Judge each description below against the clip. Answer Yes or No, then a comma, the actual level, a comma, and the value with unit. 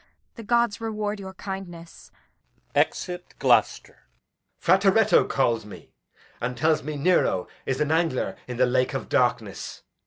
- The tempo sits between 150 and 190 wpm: No, slow, 135 wpm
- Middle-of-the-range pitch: Yes, medium, 170 Hz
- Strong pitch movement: Yes, wide, 7.2 semitones